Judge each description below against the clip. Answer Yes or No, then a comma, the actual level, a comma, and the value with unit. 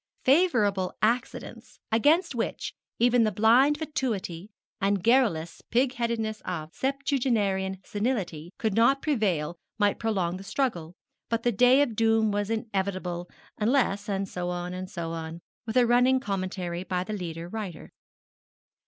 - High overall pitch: Yes, high, 210 Hz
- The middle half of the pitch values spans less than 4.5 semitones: No, average, 4.9 semitones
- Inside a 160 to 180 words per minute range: No, average, 140 wpm